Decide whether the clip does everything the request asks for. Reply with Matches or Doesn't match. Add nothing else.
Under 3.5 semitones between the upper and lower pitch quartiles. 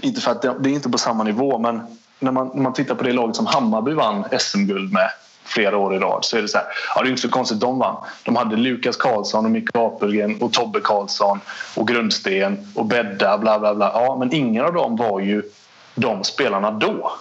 Doesn't match